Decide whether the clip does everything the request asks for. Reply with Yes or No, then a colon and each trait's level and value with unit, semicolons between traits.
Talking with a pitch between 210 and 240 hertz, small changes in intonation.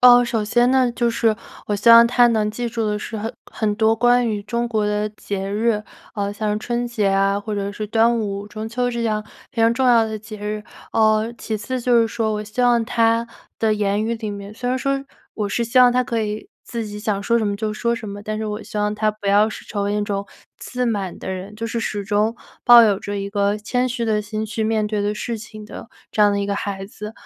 Yes: high, 215 Hz; narrow, 2.0 semitones